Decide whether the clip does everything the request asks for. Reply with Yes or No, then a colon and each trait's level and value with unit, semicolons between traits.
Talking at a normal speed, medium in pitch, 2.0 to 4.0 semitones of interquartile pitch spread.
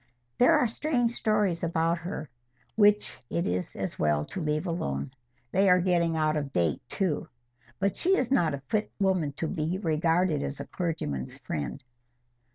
No: average, 165 wpm; medium, 170 Hz; average, 4.5 semitones